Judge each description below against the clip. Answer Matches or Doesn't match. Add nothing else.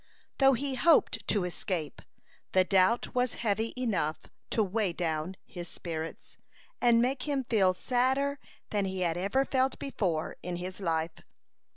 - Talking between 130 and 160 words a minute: Matches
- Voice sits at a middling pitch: Doesn't match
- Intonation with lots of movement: Matches